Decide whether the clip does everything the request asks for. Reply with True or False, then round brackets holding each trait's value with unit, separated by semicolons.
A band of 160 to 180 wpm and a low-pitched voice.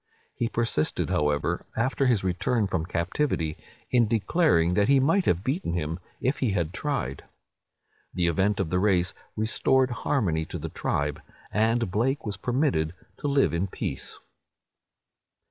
False (145 wpm; 105 Hz)